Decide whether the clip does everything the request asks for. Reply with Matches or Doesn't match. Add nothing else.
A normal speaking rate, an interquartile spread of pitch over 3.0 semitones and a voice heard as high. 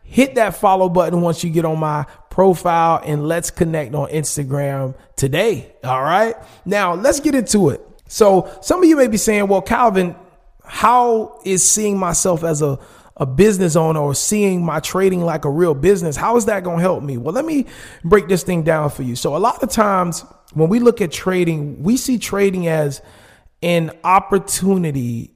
Doesn't match